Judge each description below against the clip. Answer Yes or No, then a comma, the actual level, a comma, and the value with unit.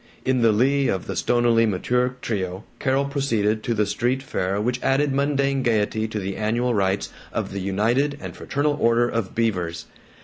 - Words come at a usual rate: Yes, average, 175 wpm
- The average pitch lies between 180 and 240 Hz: No, low, 115 Hz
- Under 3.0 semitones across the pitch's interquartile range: No, average, 4.2 semitones